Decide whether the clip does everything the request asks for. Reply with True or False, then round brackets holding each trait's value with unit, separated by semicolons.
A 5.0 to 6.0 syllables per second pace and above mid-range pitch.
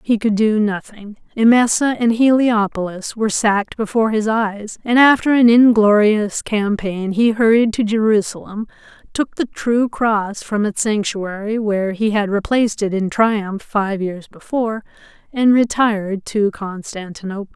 False (4.5 syllables/s; 215 Hz)